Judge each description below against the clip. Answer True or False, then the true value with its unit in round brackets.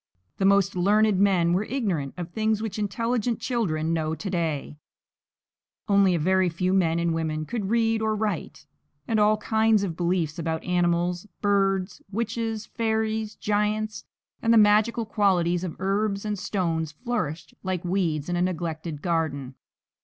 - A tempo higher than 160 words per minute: False (155 wpm)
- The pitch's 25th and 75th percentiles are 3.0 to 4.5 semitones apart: True (4.1 semitones)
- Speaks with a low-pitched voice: False (195 Hz)